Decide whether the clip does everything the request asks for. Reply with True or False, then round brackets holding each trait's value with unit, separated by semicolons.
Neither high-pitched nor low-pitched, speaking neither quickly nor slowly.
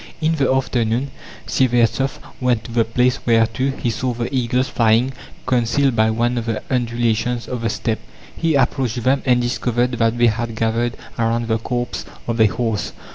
False (120 Hz; 175 wpm)